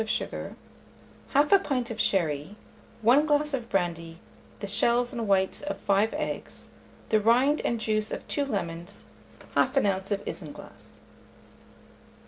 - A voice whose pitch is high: Yes, high, 220 Hz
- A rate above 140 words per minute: No, slow, 135 wpm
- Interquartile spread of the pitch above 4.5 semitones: Yes, average, 5.0 semitones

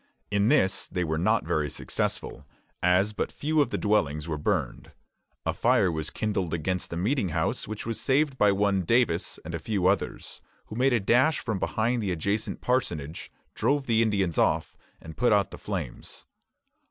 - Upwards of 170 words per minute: Yes, average, 180 wpm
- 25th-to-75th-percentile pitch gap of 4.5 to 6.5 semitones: Yes, average, 5.2 semitones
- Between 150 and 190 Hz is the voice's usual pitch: No, low, 100 Hz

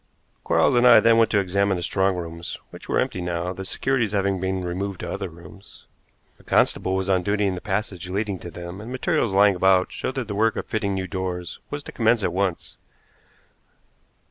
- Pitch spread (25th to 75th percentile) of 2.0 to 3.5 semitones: Yes, narrow, 2.6 semitones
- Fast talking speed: Yes, fast, 210 wpm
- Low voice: Yes, very low, 95 Hz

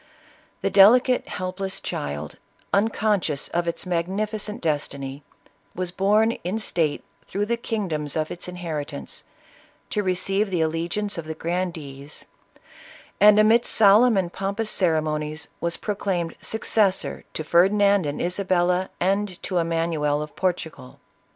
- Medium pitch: Yes, medium, 180 Hz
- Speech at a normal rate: No, slow, 130 wpm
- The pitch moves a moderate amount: Yes, average, 4.2 semitones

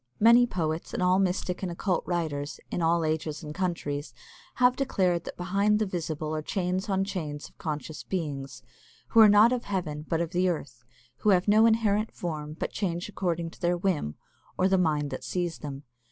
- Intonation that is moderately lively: Yes, average, 3.9 semitones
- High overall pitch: No, medium, 175 Hz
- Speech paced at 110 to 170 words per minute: No, average, 195 wpm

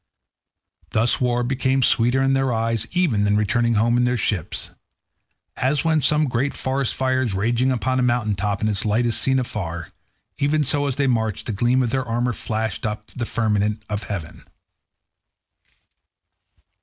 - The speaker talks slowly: No, average, 175 wpm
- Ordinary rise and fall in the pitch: Yes, average, 3.4 semitones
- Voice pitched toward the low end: Yes, low, 120 Hz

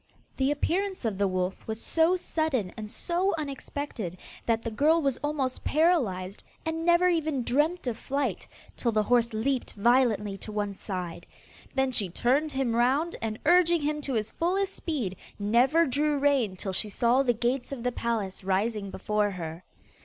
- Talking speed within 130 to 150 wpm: No, average, 170 wpm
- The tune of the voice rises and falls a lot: Yes, wide, 6.2 semitones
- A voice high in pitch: Yes, very high, 250 Hz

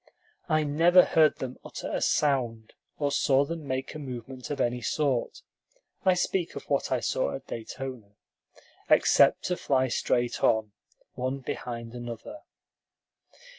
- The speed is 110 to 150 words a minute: Yes, average, 140 wpm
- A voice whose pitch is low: Yes, low, 130 Hz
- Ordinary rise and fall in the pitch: Yes, average, 4.0 semitones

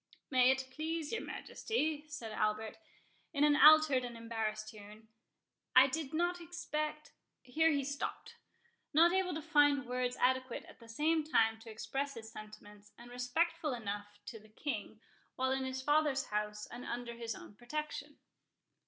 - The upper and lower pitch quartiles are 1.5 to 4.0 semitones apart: No, average, 5.3 semitones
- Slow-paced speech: No, average, 160 wpm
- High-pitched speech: Yes, very high, 260 Hz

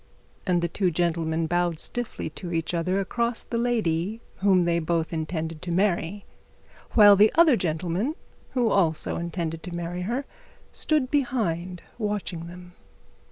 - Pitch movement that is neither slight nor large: Yes, average, 4.0 semitones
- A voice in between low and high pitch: Yes, medium, 180 Hz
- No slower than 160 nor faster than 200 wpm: No, average, 140 wpm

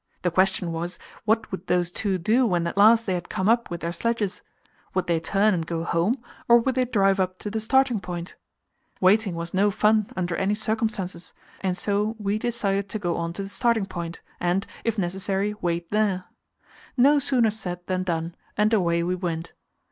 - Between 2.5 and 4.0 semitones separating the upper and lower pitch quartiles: Yes, average, 3.6 semitones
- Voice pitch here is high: Yes, high, 195 Hz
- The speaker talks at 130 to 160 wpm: No, average, 195 wpm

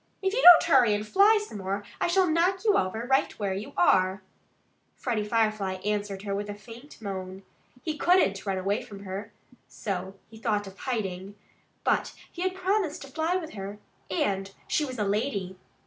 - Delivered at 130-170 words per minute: No, average, 185 wpm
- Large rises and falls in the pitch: Yes, wide, 7.7 semitones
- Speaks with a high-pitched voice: Yes, high, 210 Hz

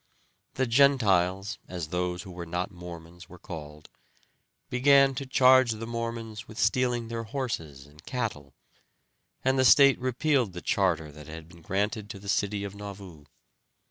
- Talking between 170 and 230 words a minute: No, average, 155 wpm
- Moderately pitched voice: No, low, 100 Hz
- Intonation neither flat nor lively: No, wide, 5.9 semitones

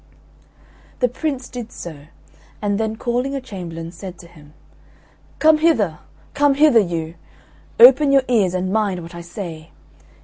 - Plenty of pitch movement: Yes, wide, 6.9 semitones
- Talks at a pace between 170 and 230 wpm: No, average, 150 wpm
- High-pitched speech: Yes, high, 205 Hz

